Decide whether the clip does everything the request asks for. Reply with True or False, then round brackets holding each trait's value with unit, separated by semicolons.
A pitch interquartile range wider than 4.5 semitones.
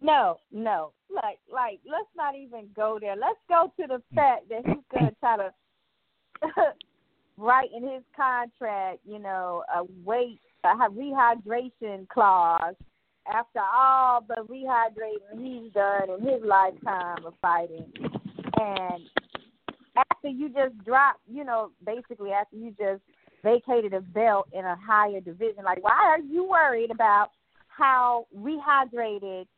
True (5.1 semitones)